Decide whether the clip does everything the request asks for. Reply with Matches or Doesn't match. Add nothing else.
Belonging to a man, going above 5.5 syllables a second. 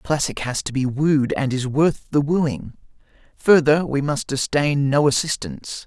Doesn't match